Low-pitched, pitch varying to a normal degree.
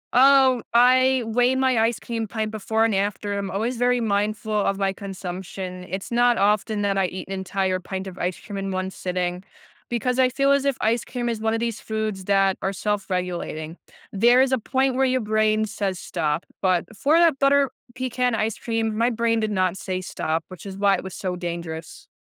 No: high, 215 Hz; average, 4.2 semitones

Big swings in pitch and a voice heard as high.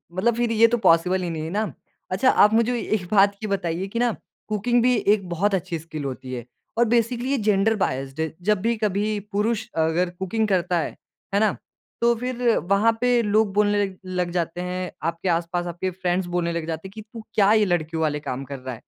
No: average, 4.5 semitones; high, 195 Hz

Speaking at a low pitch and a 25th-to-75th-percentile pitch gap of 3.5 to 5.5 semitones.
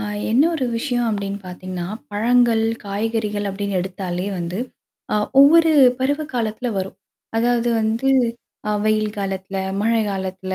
No: high, 210 Hz; average, 3.8 semitones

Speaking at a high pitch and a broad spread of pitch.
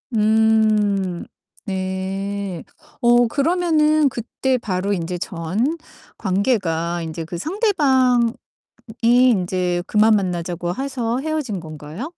Yes: high, 210 Hz; wide, 5.9 semitones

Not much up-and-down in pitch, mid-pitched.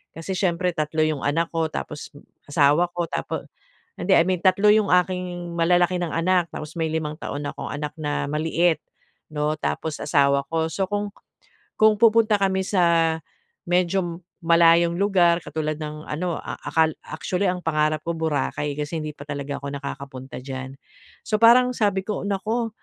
No: average, 3.3 semitones; medium, 165 Hz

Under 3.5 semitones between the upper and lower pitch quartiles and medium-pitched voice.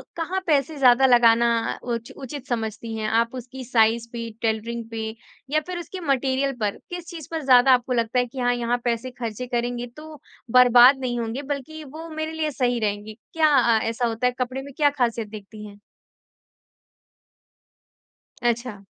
No: average, 3.0 semitones; high, 245 Hz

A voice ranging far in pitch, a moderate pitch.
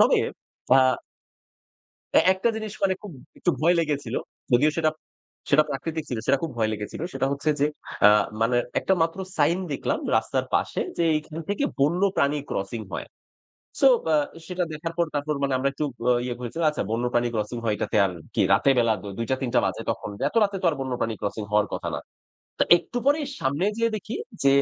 Yes: wide, 5.7 semitones; medium, 145 Hz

